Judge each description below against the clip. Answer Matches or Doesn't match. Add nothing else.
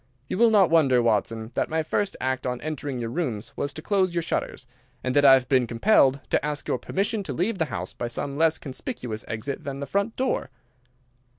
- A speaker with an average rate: Doesn't match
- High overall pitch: Doesn't match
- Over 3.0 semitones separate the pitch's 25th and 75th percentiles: Matches